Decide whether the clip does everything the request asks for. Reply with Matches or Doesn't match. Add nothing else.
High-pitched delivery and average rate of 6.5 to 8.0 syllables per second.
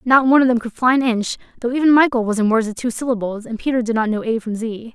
Matches